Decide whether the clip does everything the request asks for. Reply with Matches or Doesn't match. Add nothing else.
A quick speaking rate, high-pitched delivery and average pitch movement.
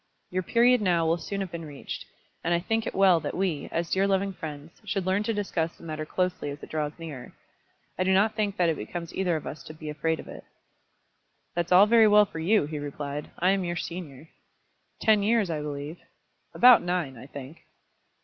Doesn't match